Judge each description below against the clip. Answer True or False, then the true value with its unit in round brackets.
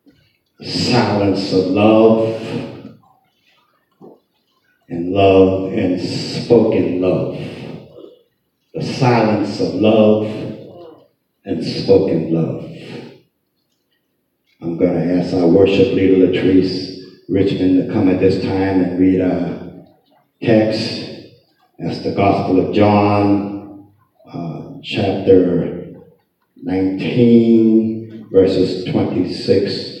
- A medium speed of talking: False (85 wpm)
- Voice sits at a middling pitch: False (95 Hz)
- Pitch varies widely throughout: False (2.8 semitones)